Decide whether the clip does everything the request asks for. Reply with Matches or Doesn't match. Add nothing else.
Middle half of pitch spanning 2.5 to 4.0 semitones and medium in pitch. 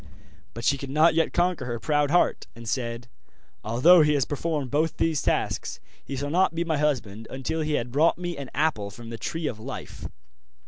Doesn't match